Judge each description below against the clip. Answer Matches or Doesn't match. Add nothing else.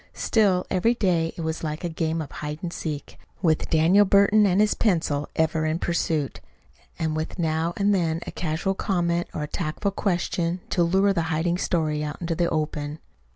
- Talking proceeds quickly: Doesn't match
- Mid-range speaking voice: Matches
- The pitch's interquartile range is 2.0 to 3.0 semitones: Matches